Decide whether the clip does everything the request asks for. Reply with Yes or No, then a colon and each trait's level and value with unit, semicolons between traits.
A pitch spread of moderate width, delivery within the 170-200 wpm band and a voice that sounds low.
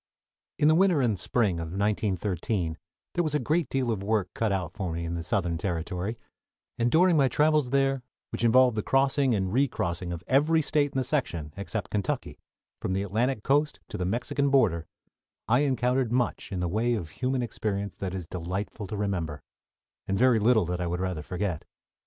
No: wide, 6.4 semitones; average, 195 wpm; low, 110 Hz